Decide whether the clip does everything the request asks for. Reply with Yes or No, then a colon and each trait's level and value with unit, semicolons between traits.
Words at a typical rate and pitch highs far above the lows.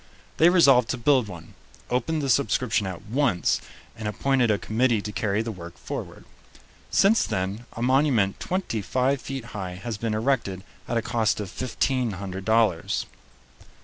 No: average, 160 wpm; average, 4.3 semitones